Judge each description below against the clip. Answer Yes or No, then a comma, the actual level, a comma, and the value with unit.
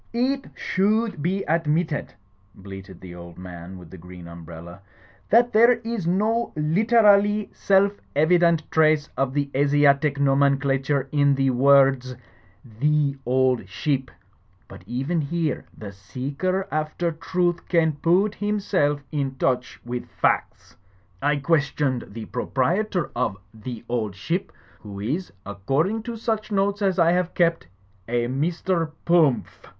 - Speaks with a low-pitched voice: No, medium, 145 Hz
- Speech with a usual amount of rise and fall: No, wide, 6.3 semitones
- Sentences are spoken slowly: No, average, 145 wpm